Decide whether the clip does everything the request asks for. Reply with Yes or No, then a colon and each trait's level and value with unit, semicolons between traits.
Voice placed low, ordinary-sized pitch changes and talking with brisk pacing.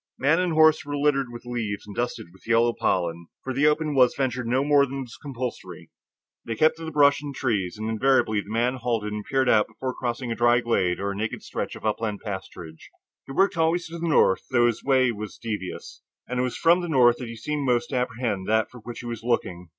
Yes: low, 120 Hz; average, 4.0 semitones; fast, 235 wpm